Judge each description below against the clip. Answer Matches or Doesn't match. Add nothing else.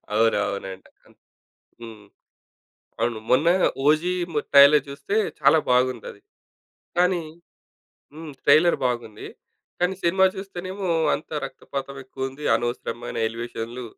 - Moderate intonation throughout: Doesn't match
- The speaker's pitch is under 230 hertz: Matches